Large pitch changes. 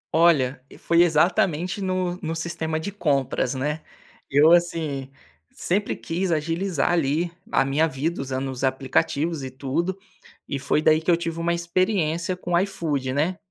No: average, 3.7 semitones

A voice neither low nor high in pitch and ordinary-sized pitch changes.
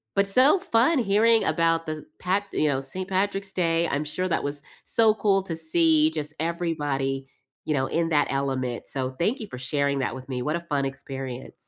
No: medium, 160 Hz; wide, 5.7 semitones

